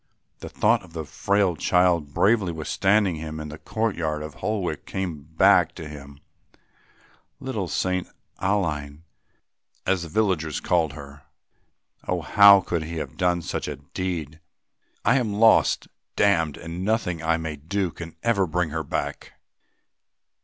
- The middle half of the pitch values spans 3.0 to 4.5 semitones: Yes, average, 3.7 semitones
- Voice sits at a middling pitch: No, very low, 85 Hz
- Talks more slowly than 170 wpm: Yes, average, 145 wpm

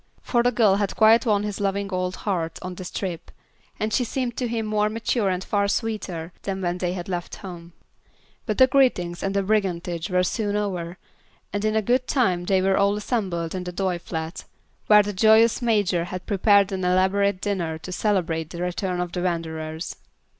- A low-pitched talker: No, high, 195 Hz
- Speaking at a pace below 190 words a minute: No, average, 195 wpm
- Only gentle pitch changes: No, average, 3.0 semitones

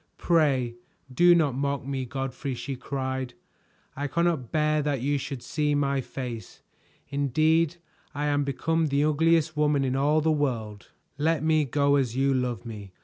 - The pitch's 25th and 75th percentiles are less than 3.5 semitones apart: Yes, average, 2.7 semitones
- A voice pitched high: No, medium, 140 Hz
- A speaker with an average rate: Yes, average, 160 wpm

